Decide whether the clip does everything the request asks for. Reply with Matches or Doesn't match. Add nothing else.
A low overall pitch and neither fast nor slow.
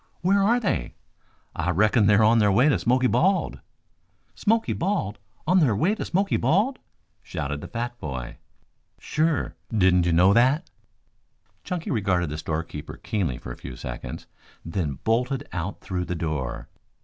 Matches